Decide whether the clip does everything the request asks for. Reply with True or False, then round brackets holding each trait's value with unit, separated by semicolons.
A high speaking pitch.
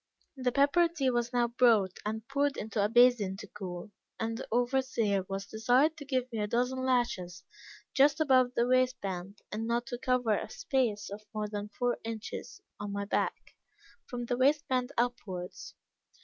True (240 Hz)